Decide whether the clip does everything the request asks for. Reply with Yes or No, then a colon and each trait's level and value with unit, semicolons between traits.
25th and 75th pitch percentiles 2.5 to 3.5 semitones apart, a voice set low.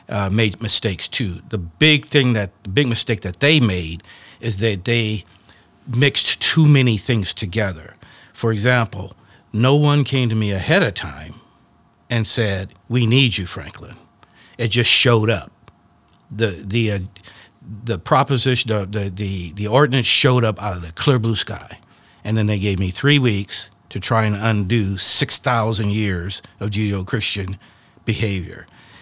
Yes: average, 3.1 semitones; low, 110 Hz